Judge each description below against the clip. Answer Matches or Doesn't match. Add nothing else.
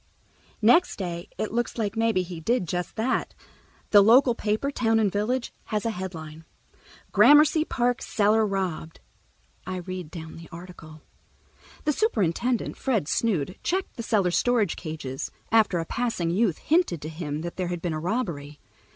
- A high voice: Matches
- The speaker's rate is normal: Matches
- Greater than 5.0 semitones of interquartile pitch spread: Matches